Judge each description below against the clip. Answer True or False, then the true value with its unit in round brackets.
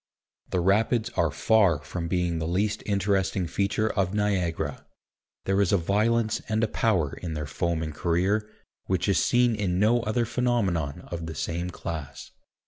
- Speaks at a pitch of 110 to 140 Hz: False (95 Hz)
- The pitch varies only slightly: False (4.3 semitones)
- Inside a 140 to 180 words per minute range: True (160 wpm)